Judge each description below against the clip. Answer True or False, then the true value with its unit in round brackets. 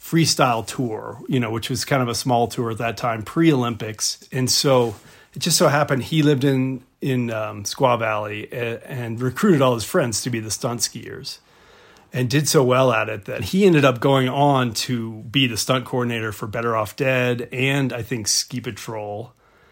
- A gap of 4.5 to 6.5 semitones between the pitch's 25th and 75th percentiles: False (3.1 semitones)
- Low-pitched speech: True (125 Hz)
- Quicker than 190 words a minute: True (200 wpm)